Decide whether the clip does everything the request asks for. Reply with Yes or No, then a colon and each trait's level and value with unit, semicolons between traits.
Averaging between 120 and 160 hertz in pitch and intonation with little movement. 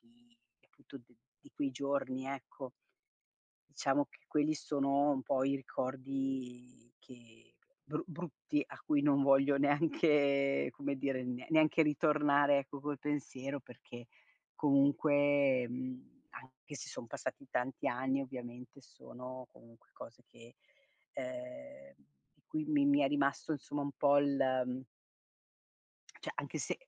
Yes: medium, 140 Hz; narrow, 2.3 semitones